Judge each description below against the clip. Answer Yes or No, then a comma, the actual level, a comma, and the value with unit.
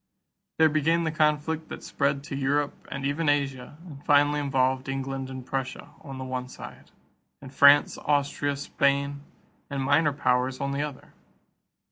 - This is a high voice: No, medium, 140 Hz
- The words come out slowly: No, average, 155 wpm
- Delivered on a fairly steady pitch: Yes, narrow, 1.6 semitones